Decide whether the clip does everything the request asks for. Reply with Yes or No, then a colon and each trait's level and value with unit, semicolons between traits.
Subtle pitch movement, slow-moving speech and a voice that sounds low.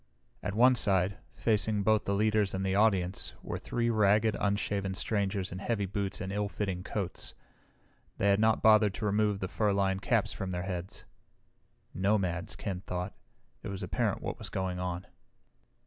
No: narrow, 2.1 semitones; average, 170 wpm; low, 100 Hz